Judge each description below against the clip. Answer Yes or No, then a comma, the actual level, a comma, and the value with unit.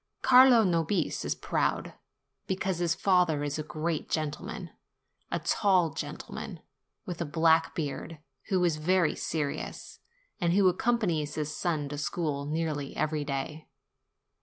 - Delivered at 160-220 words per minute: No, slow, 135 wpm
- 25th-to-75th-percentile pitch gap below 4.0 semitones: Yes, average, 3.0 semitones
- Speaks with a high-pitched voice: No, medium, 160 Hz